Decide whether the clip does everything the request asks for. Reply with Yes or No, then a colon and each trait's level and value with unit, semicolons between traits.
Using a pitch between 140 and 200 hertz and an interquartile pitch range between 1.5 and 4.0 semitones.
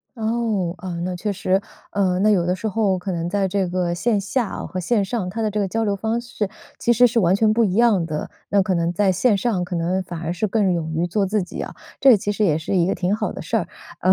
Yes: high, 195 Hz; average, 3.3 semitones